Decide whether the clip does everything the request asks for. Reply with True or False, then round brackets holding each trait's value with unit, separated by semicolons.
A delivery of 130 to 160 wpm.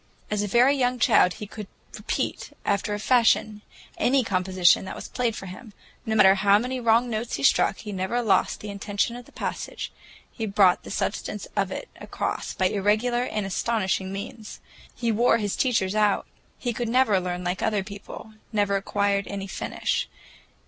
False (180 wpm)